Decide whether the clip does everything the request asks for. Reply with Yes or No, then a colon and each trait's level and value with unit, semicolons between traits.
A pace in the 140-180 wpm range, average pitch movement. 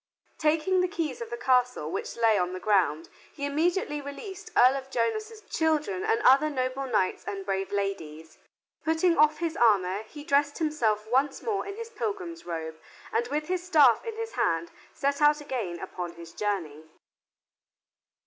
No: average, 170 wpm; wide, 8.8 semitones